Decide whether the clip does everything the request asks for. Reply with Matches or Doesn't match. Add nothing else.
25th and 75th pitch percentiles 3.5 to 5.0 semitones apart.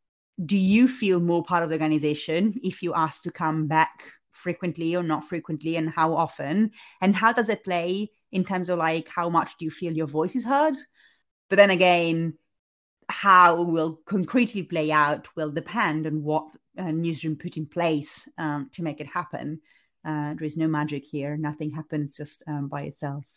Doesn't match